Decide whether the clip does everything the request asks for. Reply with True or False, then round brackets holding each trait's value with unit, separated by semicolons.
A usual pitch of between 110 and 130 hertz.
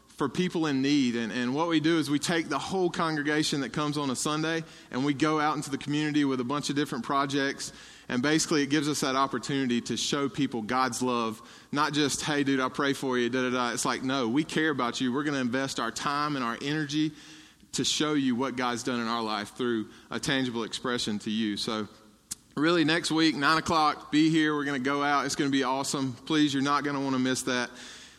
False (140 Hz)